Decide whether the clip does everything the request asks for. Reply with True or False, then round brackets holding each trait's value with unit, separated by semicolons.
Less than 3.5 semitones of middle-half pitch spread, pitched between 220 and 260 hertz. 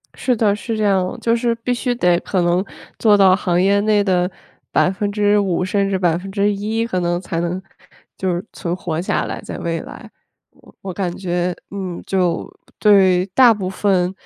False (2.5 semitones; 190 Hz)